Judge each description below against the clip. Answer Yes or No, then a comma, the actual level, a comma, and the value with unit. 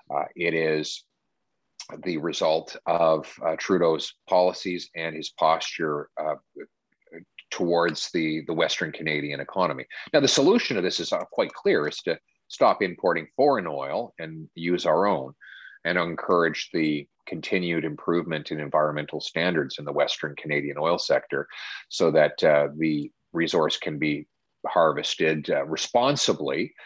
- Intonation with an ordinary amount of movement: No, narrow, 2.1 semitones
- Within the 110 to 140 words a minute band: Yes, slow, 135 wpm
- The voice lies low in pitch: Yes, very low, 80 Hz